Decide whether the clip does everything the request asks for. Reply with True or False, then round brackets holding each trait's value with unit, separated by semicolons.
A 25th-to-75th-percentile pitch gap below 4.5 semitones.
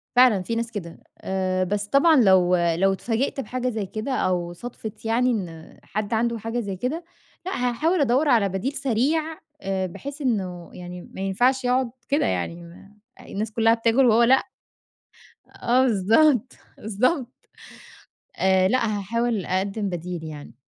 False (4.9 semitones)